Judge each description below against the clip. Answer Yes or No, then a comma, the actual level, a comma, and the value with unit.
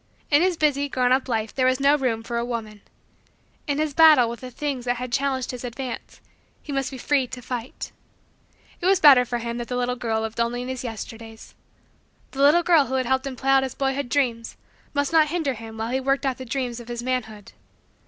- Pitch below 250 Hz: No, very high, 255 Hz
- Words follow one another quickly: Yes, fast, 225 wpm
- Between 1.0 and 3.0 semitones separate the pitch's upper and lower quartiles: Yes, average, 2.7 semitones